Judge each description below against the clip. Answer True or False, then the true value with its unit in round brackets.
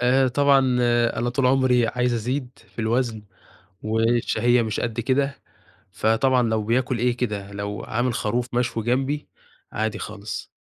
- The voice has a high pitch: False (120 Hz)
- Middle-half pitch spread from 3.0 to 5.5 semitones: False (2.4 semitones)